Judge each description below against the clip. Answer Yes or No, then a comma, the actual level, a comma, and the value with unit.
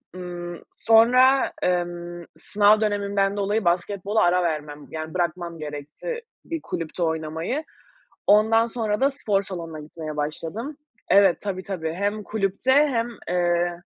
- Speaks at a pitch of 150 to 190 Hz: Yes, medium, 185 Hz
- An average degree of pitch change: Yes, average, 4.0 semitones